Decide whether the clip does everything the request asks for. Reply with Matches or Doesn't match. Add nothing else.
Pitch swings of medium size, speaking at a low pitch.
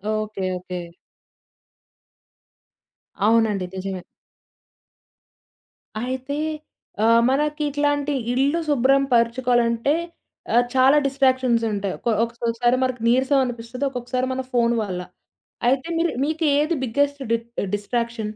Doesn't match